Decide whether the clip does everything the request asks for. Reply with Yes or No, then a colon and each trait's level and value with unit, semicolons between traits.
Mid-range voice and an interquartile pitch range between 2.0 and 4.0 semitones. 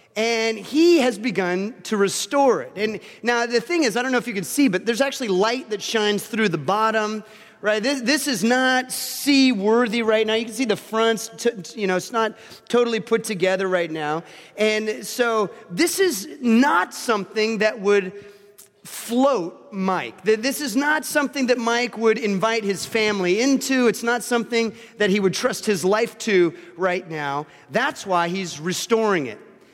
No: high, 220 Hz; average, 3.3 semitones